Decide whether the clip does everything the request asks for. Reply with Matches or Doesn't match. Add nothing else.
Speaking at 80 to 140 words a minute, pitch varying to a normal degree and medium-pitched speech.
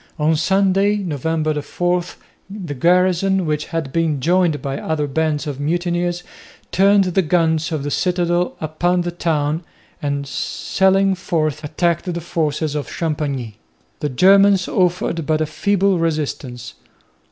Matches